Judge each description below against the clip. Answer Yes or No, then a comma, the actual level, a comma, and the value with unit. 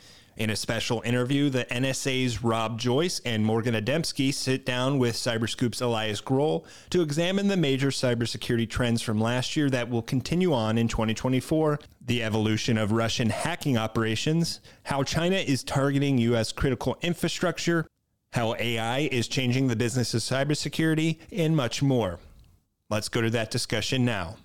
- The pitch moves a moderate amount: Yes, average, 3.7 semitones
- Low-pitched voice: Yes, low, 125 Hz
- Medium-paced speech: Yes, average, 150 wpm